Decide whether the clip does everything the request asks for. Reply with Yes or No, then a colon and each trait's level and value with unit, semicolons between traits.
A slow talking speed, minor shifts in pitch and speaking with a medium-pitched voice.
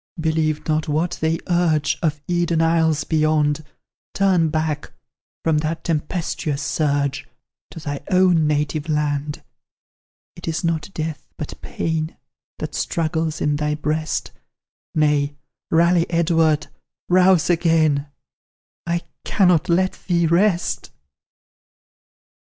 Yes: slow, 110 wpm; narrow, 2.1 semitones; medium, 160 Hz